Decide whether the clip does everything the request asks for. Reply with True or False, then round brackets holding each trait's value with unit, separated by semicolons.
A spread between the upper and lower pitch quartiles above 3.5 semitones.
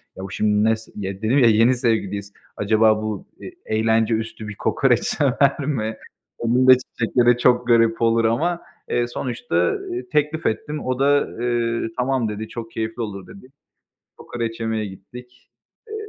False (2.5 semitones)